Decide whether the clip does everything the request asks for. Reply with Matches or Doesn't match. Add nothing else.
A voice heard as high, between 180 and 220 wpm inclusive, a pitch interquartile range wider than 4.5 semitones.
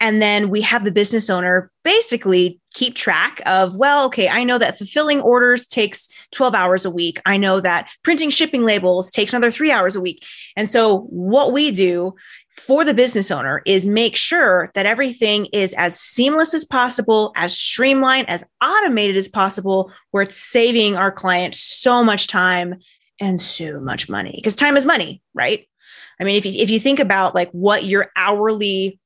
Matches